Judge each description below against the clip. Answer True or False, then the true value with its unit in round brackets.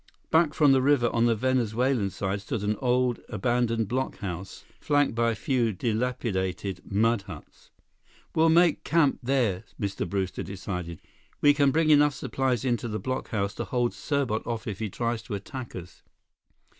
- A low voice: True (120 Hz)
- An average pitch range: True (4.6 semitones)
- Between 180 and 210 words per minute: False (160 wpm)